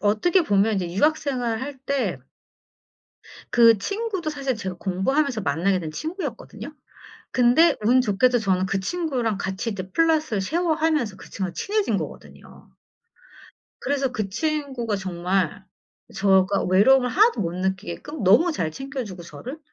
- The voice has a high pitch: Yes, high, 230 Hz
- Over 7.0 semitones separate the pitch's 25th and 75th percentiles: Yes, wide, 7.4 semitones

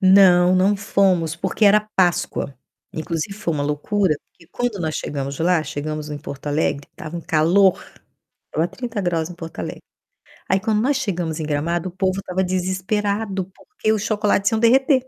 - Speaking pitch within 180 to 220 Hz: Yes, medium, 185 Hz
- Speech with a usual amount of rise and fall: Yes, average, 4.2 semitones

